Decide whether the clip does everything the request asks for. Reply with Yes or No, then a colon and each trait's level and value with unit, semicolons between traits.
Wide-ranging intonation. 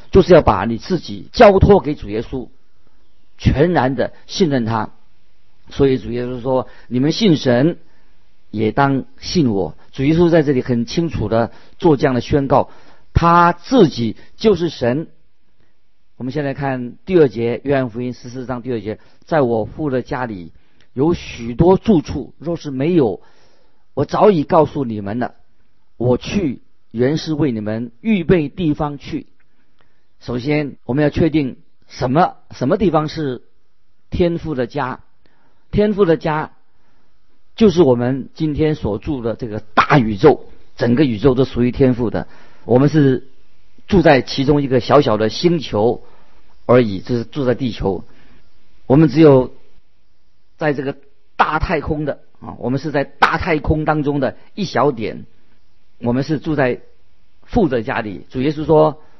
No: average, 5.0 semitones